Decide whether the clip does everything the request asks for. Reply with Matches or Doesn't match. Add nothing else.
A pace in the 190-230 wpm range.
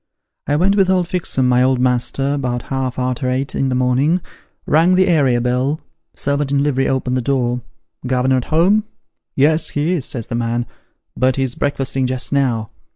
Matches